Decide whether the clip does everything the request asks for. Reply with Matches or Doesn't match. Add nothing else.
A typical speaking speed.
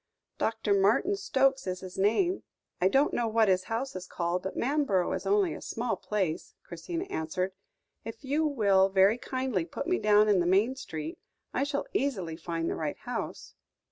Matches